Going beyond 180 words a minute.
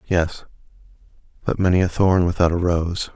No: average, 150 wpm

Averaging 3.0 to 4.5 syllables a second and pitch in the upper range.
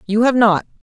No: 5.5 syllables/s; high, 220 Hz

